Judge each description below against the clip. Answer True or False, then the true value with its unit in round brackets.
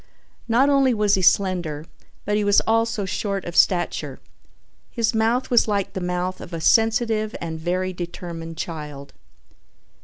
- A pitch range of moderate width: True (4.4 semitones)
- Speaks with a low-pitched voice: False (190 Hz)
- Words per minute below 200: True (150 wpm)